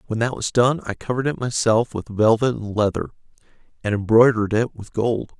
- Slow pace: No, average, 190 wpm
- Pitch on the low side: Yes, low, 115 Hz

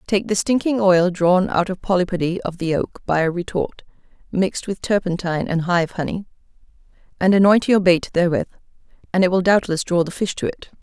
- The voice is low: No, medium, 185 Hz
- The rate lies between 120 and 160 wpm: No, average, 190 wpm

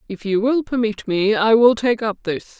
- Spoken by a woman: Yes, female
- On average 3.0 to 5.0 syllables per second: Yes, 4.7 syllables/s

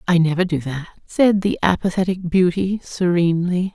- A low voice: No, medium, 180 Hz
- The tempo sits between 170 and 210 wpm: No, average, 145 wpm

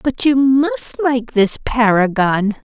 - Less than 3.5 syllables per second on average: Yes, 3.2 syllables/s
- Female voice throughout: Yes, female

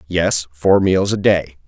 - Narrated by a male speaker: Yes, male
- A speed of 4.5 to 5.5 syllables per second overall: No, 3.9 syllables/s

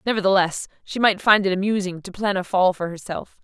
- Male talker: No, female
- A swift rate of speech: Yes, fast, 210 wpm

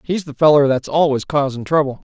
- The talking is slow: No, average, 200 wpm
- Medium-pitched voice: Yes, medium, 145 Hz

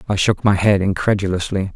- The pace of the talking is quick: No, average, 170 wpm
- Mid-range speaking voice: No, very low, 95 Hz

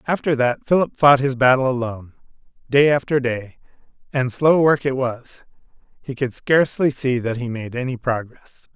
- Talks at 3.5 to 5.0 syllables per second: Yes, 4.9 syllables/s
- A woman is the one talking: No, male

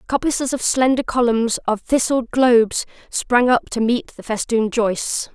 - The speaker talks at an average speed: Yes, average, 155 wpm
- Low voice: No, high, 240 Hz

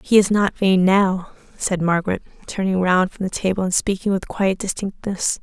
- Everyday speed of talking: Yes, average, 190 wpm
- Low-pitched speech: No, high, 190 Hz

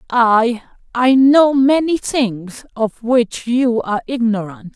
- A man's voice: No, female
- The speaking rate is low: Yes, slow, 115 wpm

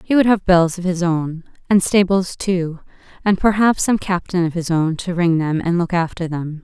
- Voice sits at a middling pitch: Yes, medium, 175 Hz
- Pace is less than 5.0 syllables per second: Yes, 4.8 syllables/s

